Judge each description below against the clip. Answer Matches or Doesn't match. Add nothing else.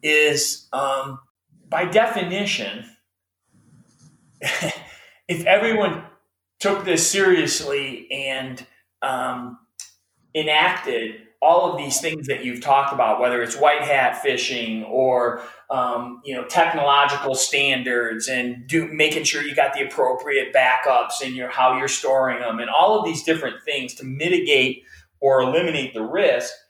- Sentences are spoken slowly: Matches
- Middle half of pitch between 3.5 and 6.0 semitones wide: Matches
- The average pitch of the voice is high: Doesn't match